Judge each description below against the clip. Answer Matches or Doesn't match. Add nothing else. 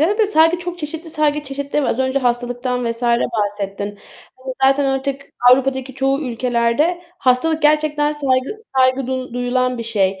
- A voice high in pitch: Matches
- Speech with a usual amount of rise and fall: Matches